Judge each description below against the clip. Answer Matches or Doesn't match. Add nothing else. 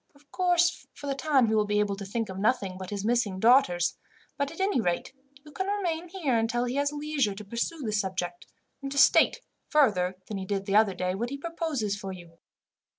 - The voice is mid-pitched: Doesn't match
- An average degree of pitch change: Doesn't match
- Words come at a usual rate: Doesn't match